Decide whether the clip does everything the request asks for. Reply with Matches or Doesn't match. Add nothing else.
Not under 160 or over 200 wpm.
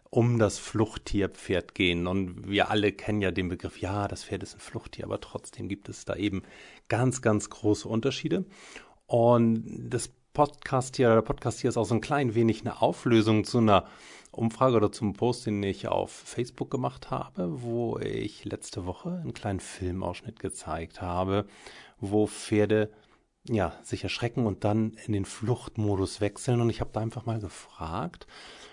Matches